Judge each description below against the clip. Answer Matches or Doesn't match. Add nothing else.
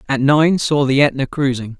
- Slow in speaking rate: Doesn't match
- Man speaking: Matches